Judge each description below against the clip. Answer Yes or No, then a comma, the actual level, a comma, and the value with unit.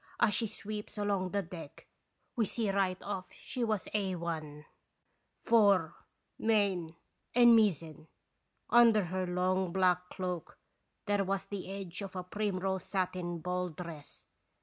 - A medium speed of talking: No, slow, 130 wpm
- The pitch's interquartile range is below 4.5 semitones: Yes, narrow, 2.4 semitones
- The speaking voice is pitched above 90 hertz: Yes, medium, 185 Hz